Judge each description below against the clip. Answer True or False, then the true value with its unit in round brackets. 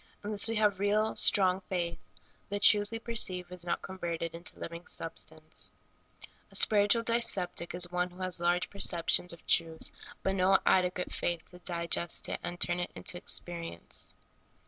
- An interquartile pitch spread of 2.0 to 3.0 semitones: True (2.7 semitones)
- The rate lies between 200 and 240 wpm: False (160 wpm)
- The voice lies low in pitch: False (180 Hz)